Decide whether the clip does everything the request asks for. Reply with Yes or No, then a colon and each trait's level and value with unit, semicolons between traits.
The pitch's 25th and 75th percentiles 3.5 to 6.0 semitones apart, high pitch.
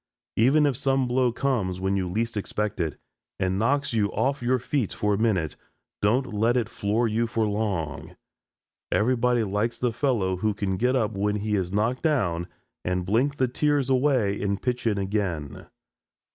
No: average, 4.1 semitones; low, 110 Hz